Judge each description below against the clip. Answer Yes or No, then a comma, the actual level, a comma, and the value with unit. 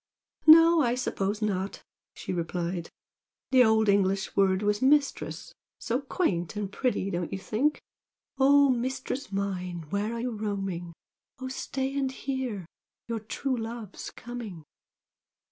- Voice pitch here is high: Yes, high, 220 Hz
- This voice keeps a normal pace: No, slow, 130 wpm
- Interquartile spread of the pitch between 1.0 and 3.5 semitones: No, average, 5.2 semitones